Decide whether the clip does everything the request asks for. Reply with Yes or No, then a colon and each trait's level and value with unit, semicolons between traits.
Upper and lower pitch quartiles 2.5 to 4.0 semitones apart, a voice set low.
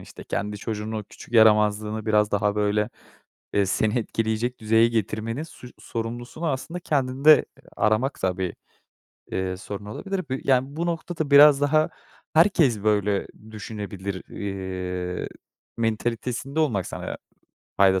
No: average, 4.5 semitones; low, 110 Hz